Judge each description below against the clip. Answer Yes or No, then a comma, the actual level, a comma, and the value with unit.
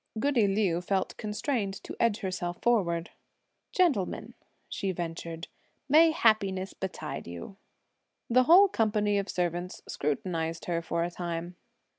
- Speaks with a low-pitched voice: No, high, 190 Hz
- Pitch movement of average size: Yes, average, 4.2 semitones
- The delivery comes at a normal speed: No, slow, 125 wpm